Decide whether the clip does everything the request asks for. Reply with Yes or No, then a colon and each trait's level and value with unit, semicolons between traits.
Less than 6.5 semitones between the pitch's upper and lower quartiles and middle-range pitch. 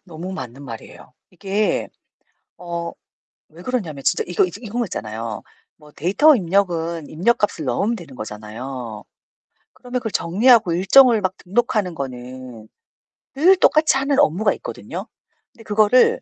No: wide, 8.4 semitones; medium, 180 Hz